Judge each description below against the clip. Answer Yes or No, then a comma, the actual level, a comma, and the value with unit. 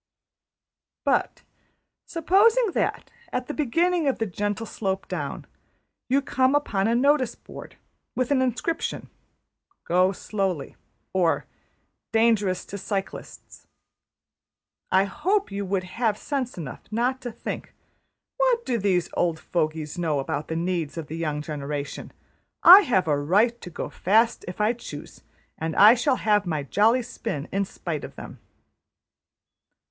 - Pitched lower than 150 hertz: No, high, 205 Hz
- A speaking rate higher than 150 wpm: No, average, 140 wpm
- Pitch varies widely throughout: Yes, wide, 6.7 semitones